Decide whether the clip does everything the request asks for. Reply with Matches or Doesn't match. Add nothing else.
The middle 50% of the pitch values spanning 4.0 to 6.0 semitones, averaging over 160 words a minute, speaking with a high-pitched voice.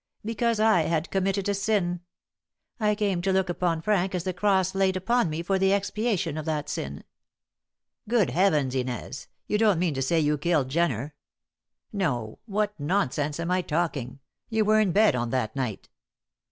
Doesn't match